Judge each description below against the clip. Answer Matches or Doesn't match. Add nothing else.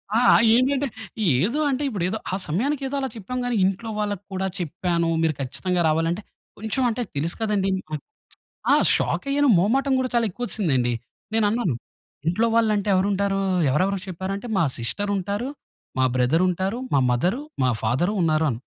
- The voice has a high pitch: Matches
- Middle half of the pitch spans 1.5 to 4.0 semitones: Doesn't match